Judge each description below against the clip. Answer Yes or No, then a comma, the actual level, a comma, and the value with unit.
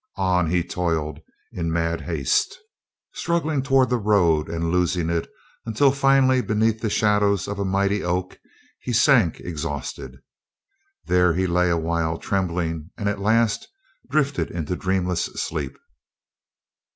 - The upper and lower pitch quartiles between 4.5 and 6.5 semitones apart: Yes, average, 5.0 semitones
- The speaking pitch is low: Yes, very low, 95 Hz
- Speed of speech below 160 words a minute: Yes, slow, 135 wpm